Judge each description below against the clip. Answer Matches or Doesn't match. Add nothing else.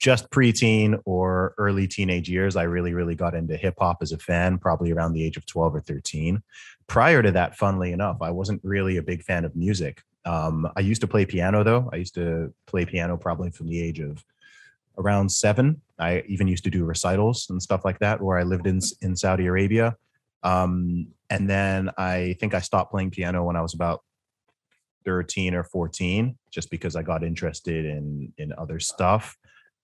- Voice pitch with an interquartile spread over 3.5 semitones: Doesn't match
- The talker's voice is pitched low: Matches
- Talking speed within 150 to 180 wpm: Doesn't match